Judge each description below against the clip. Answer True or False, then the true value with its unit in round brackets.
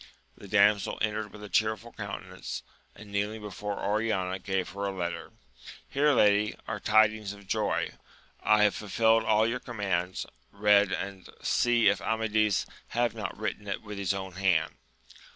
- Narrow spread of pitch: True (1.7 semitones)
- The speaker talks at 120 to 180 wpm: True (160 wpm)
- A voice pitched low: True (105 Hz)